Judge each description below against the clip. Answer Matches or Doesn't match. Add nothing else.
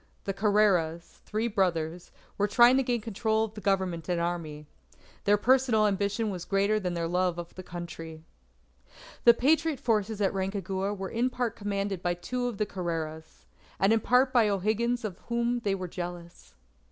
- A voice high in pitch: Matches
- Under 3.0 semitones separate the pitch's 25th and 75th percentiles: Doesn't match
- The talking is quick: Doesn't match